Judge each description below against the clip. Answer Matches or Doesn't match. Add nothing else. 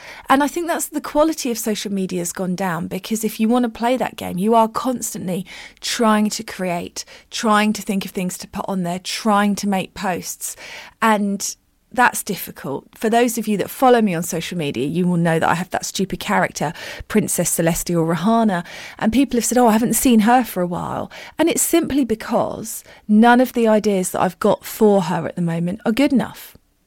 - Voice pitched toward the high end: Matches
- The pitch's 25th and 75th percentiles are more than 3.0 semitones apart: Matches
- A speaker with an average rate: Doesn't match